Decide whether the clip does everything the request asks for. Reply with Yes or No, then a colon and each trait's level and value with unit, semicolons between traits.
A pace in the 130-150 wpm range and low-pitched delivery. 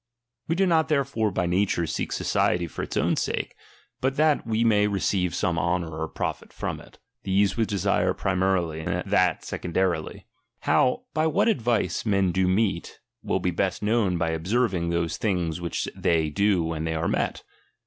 No: average, 170 wpm; very low, 95 Hz